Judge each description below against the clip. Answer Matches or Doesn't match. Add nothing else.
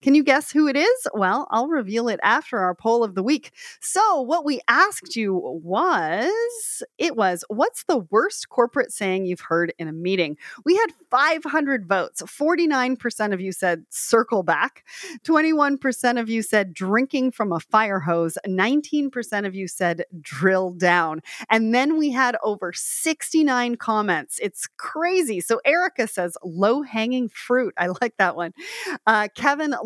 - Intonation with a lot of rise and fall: Matches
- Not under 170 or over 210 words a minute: Doesn't match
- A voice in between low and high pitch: Doesn't match